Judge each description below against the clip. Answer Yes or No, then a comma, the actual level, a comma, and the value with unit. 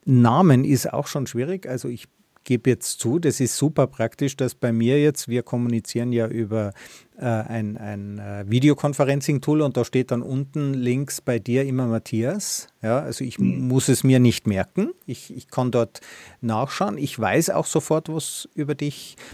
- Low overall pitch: Yes, low, 130 Hz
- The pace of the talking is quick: No, average, 180 wpm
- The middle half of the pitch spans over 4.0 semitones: No, average, 3.6 semitones